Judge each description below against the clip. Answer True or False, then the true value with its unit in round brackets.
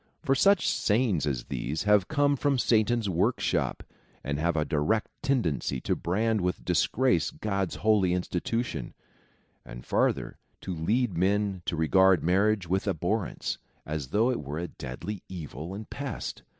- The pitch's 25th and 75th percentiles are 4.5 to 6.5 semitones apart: True (5.1 semitones)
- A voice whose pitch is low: True (95 Hz)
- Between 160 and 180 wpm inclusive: False (150 wpm)